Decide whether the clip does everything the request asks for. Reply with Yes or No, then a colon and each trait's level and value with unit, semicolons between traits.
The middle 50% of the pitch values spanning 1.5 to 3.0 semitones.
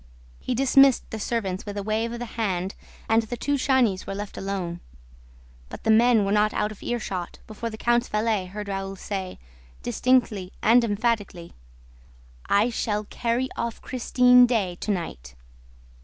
No: average, 3.4 semitones